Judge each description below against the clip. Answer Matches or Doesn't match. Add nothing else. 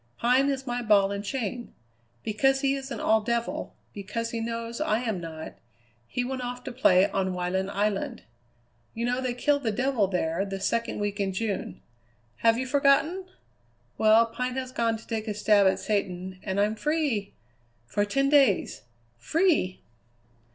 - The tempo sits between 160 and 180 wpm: Matches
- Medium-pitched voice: Doesn't match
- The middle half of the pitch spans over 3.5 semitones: Matches